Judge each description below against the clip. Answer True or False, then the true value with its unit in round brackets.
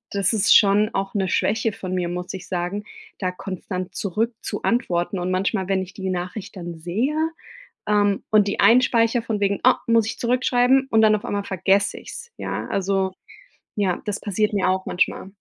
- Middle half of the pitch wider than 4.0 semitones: False (2.9 semitones)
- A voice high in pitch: True (200 Hz)